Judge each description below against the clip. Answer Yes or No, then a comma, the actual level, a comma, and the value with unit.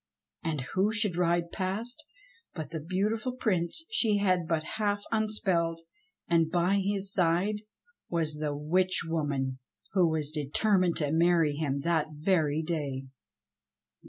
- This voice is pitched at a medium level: Yes, medium, 170 Hz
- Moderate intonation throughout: Yes, average, 4.2 semitones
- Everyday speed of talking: No, slow, 130 wpm